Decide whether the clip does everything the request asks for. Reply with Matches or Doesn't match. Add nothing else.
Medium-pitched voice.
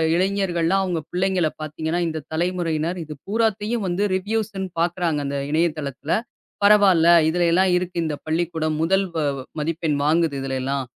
Matches